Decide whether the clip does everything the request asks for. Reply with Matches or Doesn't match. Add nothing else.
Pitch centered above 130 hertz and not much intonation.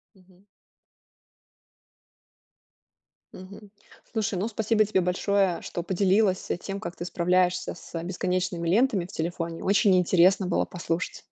Matches